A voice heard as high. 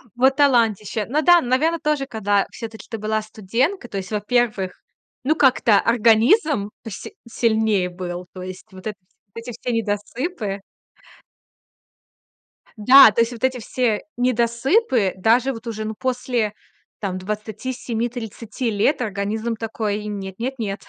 Yes: high, 225 Hz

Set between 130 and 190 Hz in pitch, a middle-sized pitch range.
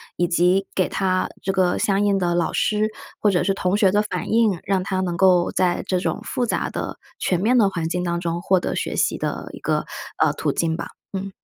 No: medium, 185 Hz; narrow, 2.1 semitones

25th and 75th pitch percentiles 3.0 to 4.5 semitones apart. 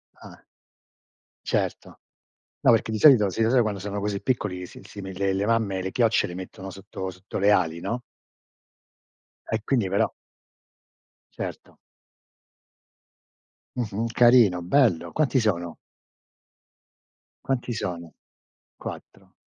Yes: average, 3.6 semitones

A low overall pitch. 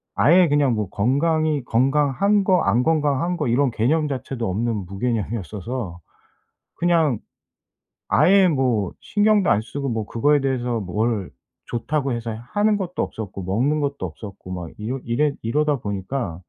Yes: low, 130 Hz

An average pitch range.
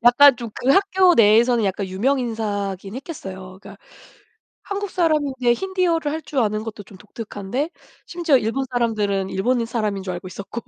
No: wide, 5.9 semitones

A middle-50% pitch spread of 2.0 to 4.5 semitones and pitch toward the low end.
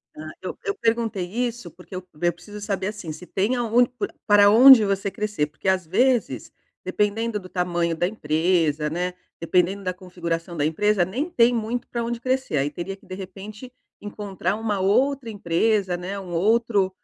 No: average, 4.2 semitones; high, 195 Hz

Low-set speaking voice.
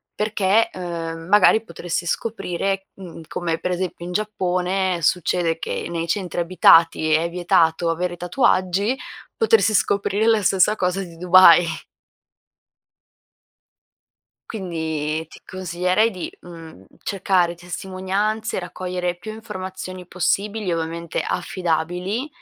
No: medium, 180 Hz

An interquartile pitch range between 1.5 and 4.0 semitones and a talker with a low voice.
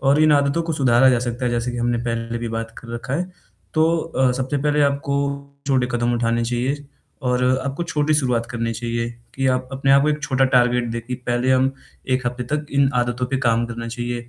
Yes: average, 2.7 semitones; low, 125 Hz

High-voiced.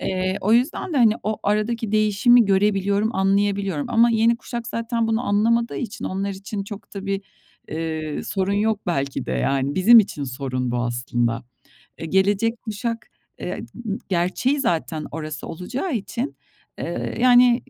Yes: high, 200 Hz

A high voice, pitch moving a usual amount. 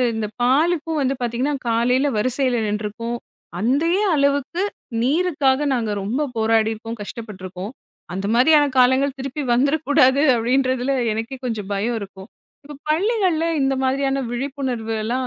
Yes: very high, 255 Hz; average, 4.0 semitones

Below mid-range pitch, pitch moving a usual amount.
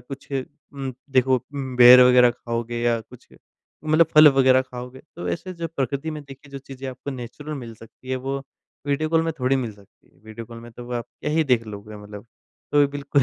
Yes: low, 130 Hz; average, 3.0 semitones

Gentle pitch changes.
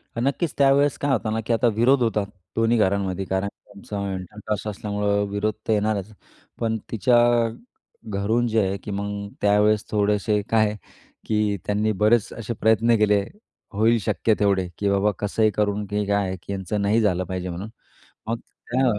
Yes: narrow, 1.9 semitones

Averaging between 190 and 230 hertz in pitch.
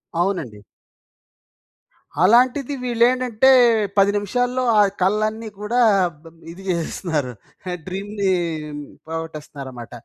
Yes: high, 200 Hz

